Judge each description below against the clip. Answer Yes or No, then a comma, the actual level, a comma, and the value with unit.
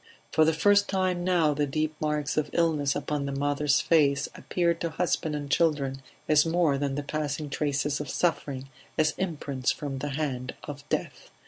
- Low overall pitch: No, medium, 150 Hz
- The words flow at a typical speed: Yes, average, 180 wpm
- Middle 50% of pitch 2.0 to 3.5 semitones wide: Yes, narrow, 2.5 semitones